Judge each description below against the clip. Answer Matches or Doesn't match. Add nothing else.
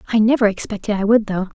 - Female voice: Matches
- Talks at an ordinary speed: Doesn't match